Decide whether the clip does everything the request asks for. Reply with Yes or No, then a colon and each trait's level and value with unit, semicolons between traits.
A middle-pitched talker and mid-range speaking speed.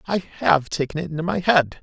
No: medium, 155 Hz; fast, 230 wpm